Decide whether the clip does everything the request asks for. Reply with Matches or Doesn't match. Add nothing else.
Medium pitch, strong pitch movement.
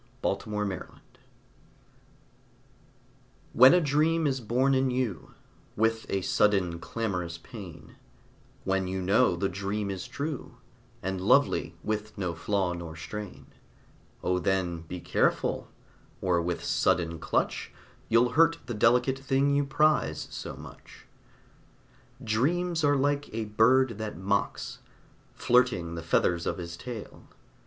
Doesn't match